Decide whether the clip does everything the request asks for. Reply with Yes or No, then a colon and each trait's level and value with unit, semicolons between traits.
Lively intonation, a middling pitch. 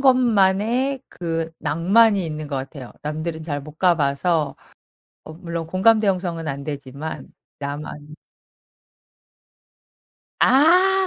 Yes: wide, 5.7 semitones; medium, 165 Hz